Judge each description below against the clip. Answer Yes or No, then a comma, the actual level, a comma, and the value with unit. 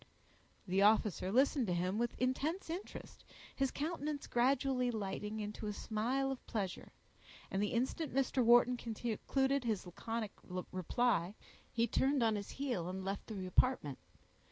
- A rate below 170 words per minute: Yes, average, 145 wpm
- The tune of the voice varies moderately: Yes, average, 4.7 semitones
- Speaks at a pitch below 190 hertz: No, high, 235 Hz